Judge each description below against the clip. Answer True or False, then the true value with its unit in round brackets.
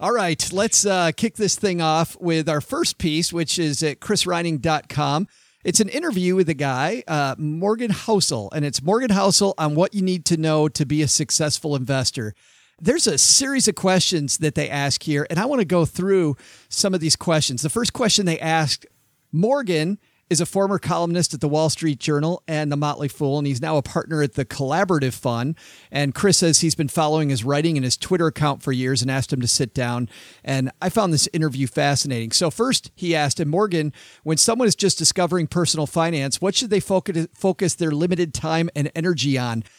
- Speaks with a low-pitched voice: False (160 Hz)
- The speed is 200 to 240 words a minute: True (205 wpm)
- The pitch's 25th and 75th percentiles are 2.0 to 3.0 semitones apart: False (4.1 semitones)